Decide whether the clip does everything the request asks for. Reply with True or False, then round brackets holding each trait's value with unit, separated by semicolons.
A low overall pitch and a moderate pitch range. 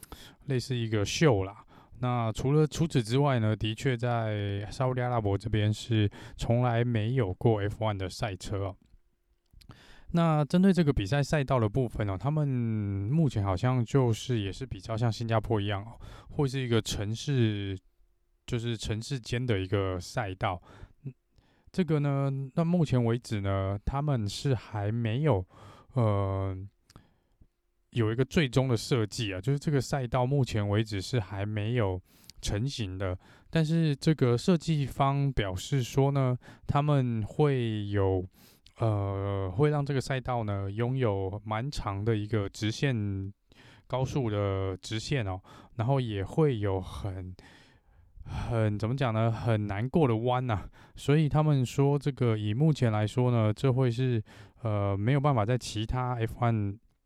True (115 Hz; 4.7 semitones)